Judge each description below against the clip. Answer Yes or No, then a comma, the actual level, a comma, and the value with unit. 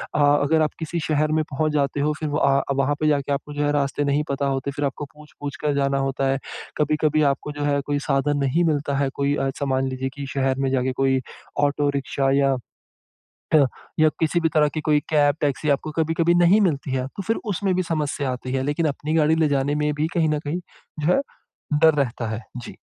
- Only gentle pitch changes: Yes, narrow, 1.9 semitones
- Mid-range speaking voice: Yes, medium, 145 Hz